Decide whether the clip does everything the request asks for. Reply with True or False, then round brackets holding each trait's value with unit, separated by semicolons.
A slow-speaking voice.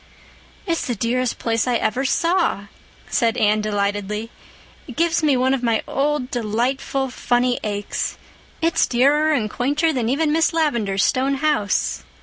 False (145 wpm)